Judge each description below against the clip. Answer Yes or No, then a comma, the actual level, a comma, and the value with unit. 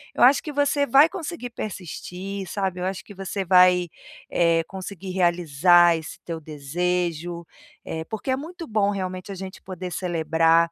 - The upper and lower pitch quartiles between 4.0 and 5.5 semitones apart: No, average, 2.9 semitones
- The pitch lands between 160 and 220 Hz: Yes, medium, 185 Hz